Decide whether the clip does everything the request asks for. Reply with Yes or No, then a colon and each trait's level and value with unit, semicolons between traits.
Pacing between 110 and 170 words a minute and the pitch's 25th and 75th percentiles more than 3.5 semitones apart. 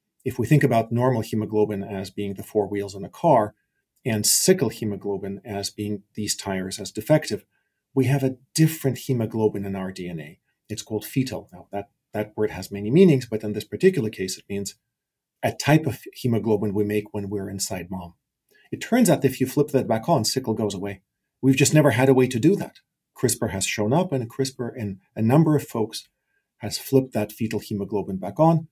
No: fast, 205 wpm; average, 4.8 semitones